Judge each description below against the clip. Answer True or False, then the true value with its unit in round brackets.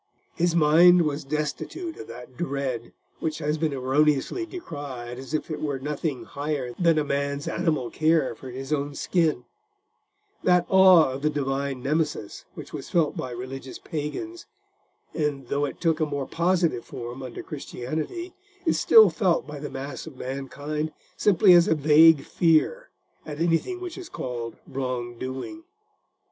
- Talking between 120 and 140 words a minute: False (155 wpm)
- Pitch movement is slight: False (3.7 semitones)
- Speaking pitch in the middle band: True (150 Hz)